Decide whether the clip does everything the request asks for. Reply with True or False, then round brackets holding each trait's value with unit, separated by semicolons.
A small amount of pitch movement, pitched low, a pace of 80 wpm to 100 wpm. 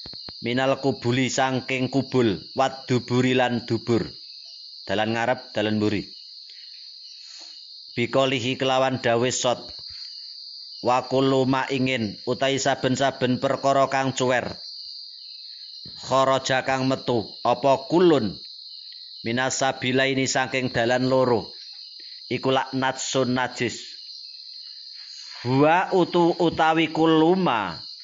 True (1.5 semitones; 130 Hz; 85 wpm)